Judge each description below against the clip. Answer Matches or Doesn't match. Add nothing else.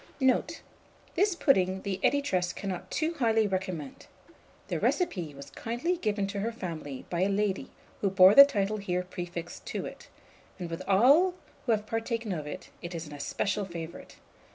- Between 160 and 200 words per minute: Matches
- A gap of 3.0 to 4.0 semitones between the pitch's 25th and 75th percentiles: Doesn't match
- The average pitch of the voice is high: Matches